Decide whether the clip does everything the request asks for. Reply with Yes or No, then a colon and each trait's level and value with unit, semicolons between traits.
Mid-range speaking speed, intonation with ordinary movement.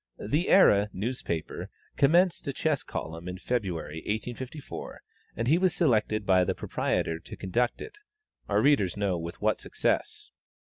No: average, 145 wpm; wide, 7.6 semitones